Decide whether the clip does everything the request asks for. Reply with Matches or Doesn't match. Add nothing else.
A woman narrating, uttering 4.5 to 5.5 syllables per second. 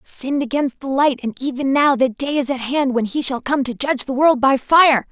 Matches